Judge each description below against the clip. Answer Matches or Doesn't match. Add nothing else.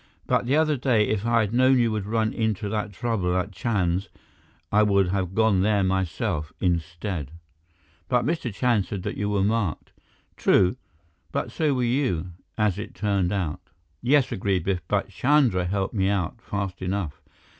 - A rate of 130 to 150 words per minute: Doesn't match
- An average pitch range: Matches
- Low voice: Matches